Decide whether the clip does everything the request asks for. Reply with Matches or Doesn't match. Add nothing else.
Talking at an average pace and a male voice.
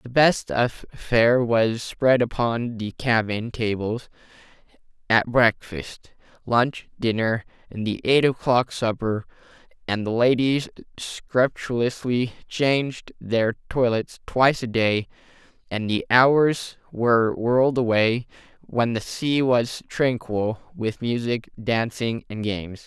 Doesn't match